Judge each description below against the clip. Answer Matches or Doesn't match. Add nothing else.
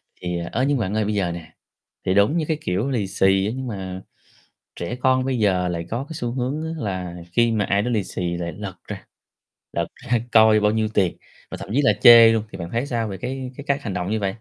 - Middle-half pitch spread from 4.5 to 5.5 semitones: Matches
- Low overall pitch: Matches